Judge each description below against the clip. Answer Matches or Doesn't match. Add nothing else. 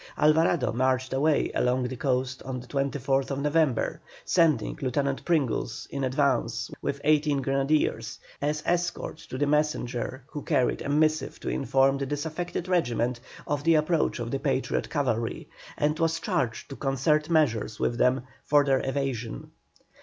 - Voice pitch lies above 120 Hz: Matches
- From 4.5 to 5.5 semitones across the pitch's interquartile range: Doesn't match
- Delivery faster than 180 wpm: Doesn't match